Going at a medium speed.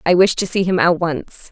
No: fast, 275 wpm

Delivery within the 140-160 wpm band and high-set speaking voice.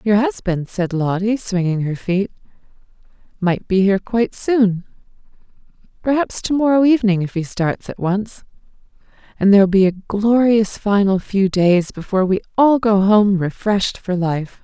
Yes: average, 150 wpm; high, 200 Hz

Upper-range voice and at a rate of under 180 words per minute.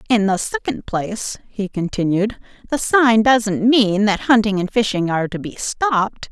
Yes: high, 215 Hz; average, 170 wpm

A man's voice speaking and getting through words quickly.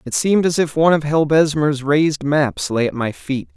Yes: male; fast, 220 wpm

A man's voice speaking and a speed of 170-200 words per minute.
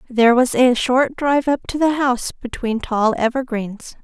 No: female; average, 180 wpm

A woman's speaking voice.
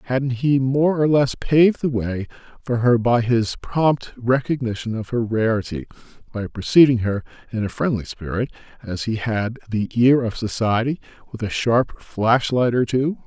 No: male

